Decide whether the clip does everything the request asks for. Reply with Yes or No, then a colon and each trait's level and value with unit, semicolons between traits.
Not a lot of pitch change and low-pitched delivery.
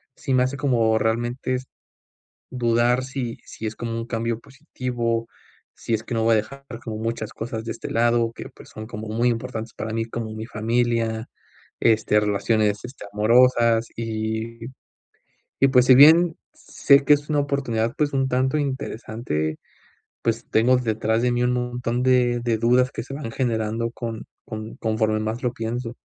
Yes: narrow, 2.1 semitones; low, 115 Hz